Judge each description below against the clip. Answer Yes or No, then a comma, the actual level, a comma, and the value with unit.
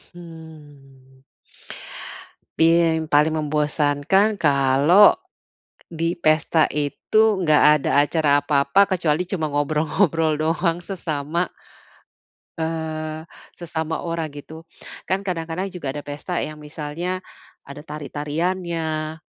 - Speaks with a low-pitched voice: No, medium, 160 Hz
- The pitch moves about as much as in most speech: No, narrow, 2.3 semitones